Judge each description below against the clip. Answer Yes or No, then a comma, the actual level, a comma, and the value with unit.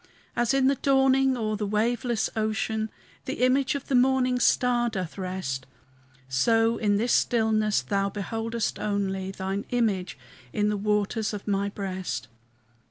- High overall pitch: Yes, high, 215 Hz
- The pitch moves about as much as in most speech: Yes, average, 3.5 semitones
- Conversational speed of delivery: Yes, average, 145 wpm